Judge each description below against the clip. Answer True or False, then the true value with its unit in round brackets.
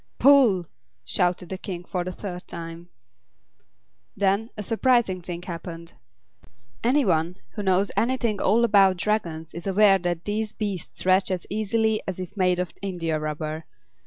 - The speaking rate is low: False (155 wpm)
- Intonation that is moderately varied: True (3.3 semitones)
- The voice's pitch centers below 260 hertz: True (185 Hz)